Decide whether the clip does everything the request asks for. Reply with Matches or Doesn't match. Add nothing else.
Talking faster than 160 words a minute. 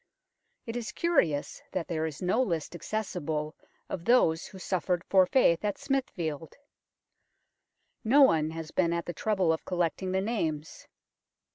Doesn't match